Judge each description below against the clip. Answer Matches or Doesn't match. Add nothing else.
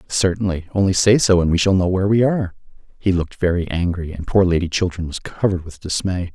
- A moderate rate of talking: Doesn't match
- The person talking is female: Doesn't match